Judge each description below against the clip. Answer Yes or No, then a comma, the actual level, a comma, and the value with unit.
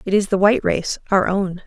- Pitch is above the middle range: Yes, high, 195 Hz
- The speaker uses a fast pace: Yes, fast, 250 wpm